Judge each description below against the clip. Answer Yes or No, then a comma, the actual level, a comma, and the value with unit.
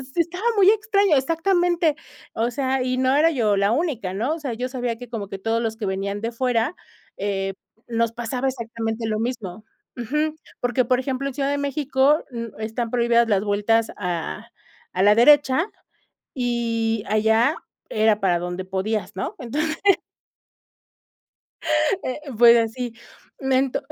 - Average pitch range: Yes, average, 3.8 semitones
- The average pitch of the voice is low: No, high, 235 Hz